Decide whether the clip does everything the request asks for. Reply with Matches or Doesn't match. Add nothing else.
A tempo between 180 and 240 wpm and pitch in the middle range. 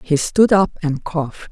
Matches